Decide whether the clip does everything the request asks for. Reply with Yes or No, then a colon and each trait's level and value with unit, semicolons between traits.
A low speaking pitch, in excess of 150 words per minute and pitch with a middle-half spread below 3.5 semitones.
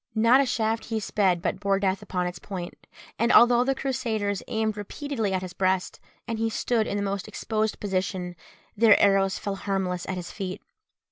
No: high, 200 Hz; average, 190 wpm; average, 3.0 semitones